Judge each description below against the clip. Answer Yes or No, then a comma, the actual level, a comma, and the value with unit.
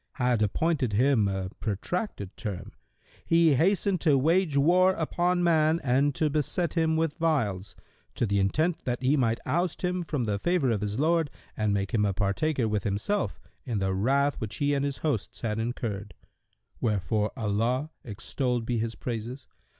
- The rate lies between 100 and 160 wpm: No, average, 170 wpm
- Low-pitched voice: Yes, low, 130 Hz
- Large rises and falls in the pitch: Yes, wide, 7.0 semitones